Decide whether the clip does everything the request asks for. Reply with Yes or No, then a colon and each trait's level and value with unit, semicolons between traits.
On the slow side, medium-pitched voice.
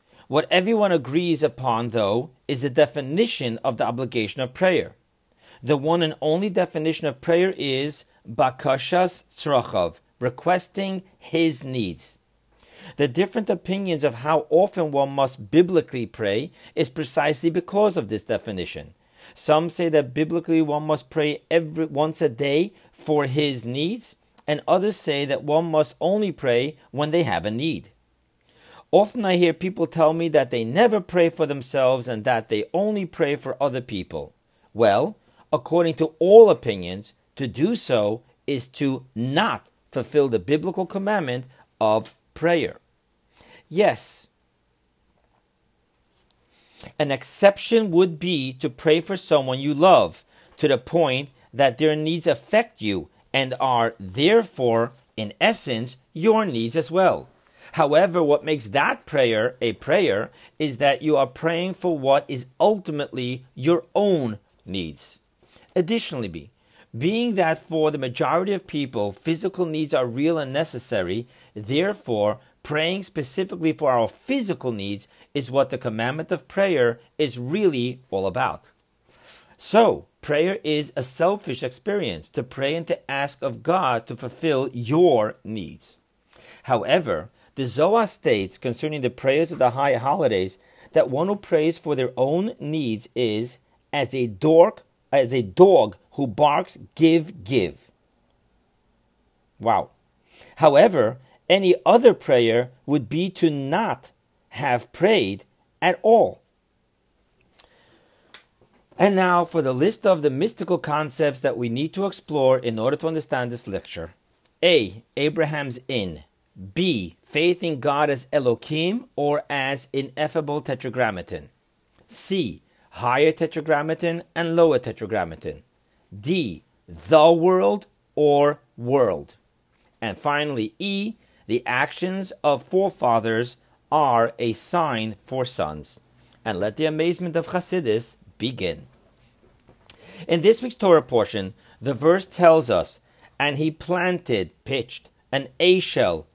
Yes: slow, 130 wpm; medium, 150 Hz